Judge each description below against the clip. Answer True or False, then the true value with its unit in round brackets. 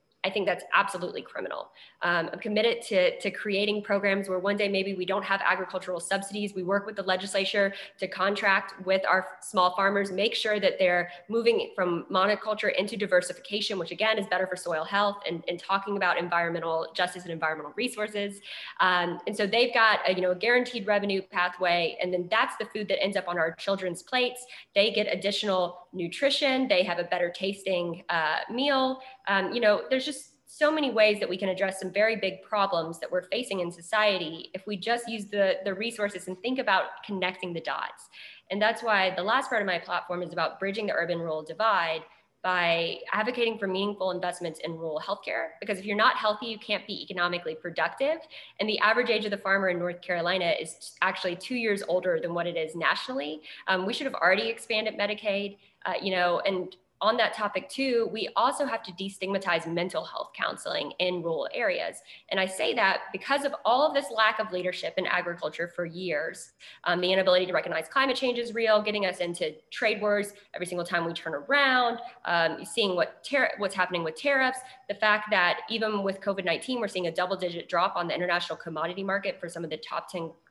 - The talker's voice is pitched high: True (195 Hz)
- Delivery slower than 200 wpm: False (205 wpm)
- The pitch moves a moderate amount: True (3.3 semitones)